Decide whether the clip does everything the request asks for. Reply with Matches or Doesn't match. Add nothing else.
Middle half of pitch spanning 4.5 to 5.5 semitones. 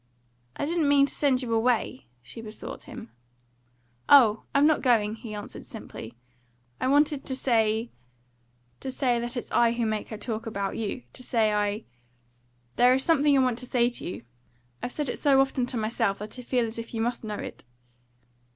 Doesn't match